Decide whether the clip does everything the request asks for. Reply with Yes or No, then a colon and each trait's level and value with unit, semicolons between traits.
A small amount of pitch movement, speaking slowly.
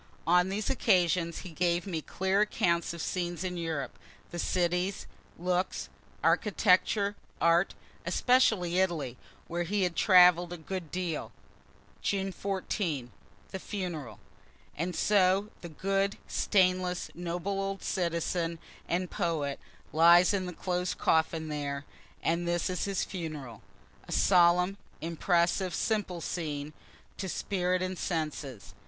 Yes: narrow, 2.2 semitones; slow, 125 wpm